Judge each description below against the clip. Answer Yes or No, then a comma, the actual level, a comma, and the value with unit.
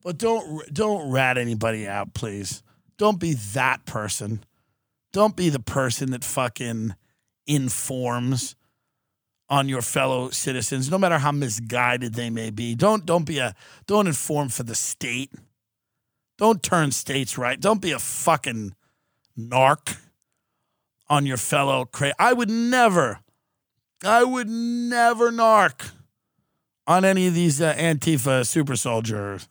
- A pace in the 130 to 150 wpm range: Yes, slow, 135 wpm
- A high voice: No, low, 135 Hz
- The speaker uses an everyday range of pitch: No, wide, 6.1 semitones